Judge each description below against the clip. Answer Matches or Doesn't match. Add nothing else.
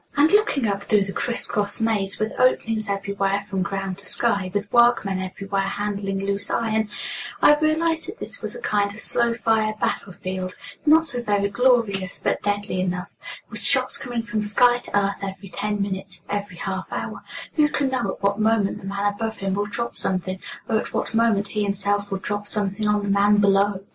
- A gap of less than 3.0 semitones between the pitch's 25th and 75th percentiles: Matches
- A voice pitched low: Doesn't match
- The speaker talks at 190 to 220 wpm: Matches